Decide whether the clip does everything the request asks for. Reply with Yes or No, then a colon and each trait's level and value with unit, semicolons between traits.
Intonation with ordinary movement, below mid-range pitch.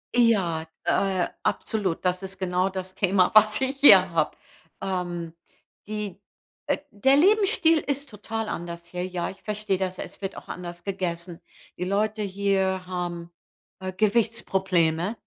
No: average, 3.0 semitones; high, 190 Hz